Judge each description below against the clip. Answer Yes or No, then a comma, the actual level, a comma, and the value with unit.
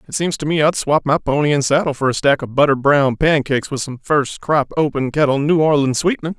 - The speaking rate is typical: No, fast, 245 wpm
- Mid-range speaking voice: Yes, medium, 145 Hz